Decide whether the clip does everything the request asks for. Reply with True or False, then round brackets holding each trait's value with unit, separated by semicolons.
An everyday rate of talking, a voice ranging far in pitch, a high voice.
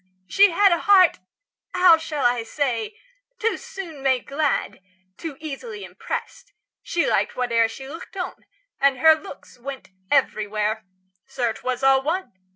True (145 wpm; 5.8 semitones; 280 Hz)